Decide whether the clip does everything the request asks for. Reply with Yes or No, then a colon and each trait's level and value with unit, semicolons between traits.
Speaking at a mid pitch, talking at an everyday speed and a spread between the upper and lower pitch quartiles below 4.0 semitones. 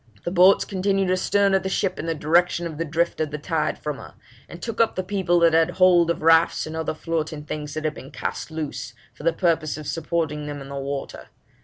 No: medium, 165 Hz; fast, 235 wpm; average, 2.8 semitones